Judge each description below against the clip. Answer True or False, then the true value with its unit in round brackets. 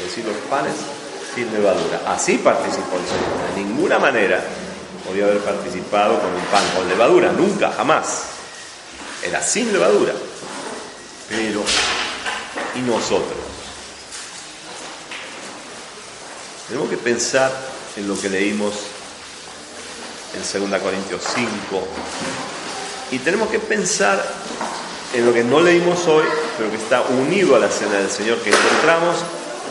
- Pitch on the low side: True (105 Hz)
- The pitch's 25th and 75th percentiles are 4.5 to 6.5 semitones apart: True (4.8 semitones)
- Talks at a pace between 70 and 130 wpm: True (125 wpm)